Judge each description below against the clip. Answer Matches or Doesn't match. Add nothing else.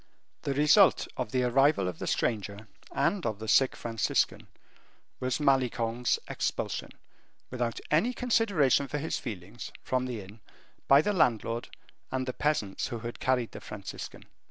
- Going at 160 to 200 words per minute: Doesn't match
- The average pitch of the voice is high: Doesn't match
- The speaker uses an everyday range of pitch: Matches